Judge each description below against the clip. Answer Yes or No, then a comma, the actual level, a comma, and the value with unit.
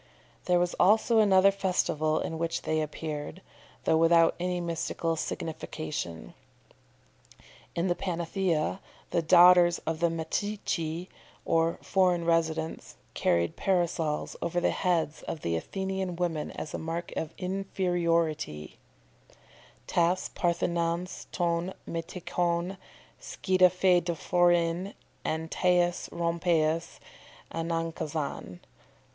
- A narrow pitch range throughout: Yes, narrow, 1.8 semitones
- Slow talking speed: Yes, slow, 95 wpm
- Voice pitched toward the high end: No, medium, 170 Hz